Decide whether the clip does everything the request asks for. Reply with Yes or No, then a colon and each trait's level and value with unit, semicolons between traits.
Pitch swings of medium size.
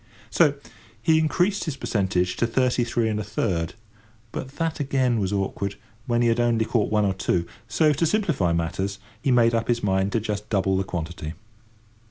Yes: average, 5.0 semitones